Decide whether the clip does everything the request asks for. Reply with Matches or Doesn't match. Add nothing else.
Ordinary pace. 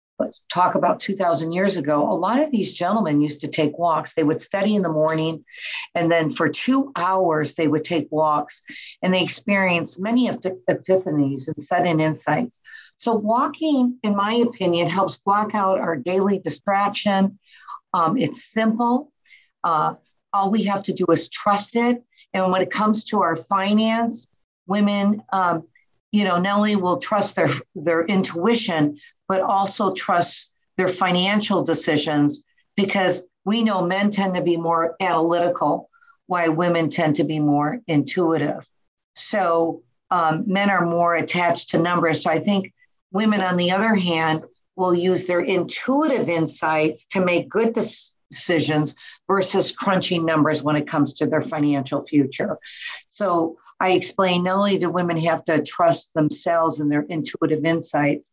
Matches